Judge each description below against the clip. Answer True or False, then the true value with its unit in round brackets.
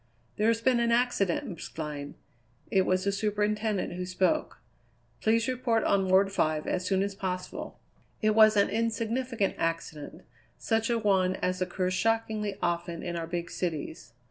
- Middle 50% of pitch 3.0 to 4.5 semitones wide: True (3.6 semitones)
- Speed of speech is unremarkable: True (155 wpm)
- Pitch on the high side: True (195 Hz)